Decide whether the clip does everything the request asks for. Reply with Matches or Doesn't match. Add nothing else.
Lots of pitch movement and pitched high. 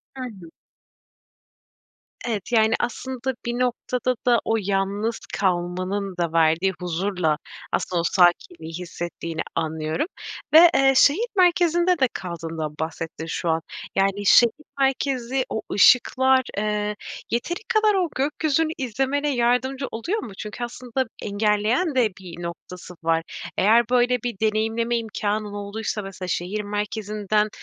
Matches